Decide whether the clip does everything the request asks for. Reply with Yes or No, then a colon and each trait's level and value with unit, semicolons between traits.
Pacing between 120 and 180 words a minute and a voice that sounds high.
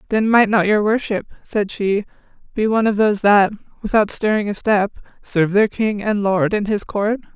No: average, 195 wpm; high, 210 Hz